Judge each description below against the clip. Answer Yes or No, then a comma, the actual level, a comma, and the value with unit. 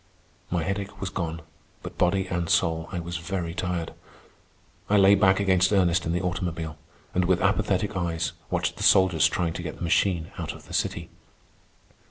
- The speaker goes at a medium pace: Yes, average, 180 wpm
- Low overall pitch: Yes, very low, 90 Hz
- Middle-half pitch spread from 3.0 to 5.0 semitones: No, narrow, 2.4 semitones